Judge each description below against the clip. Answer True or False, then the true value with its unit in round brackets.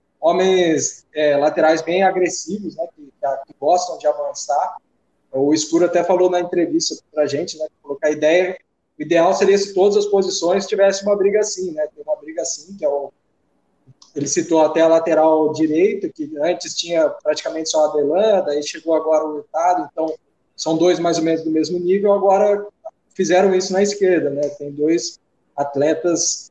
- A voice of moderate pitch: True (170 Hz)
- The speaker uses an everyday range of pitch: True (3.7 semitones)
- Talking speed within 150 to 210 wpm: True (185 wpm)